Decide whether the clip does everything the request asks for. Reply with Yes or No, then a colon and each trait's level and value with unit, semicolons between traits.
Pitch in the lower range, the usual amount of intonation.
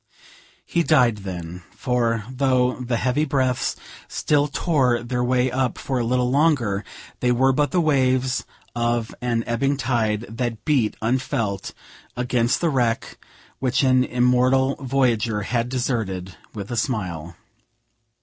No: low, 125 Hz; narrow, 2.3 semitones